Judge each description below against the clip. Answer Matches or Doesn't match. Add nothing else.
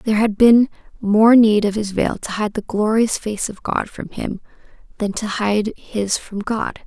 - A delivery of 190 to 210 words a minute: Matches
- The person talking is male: Doesn't match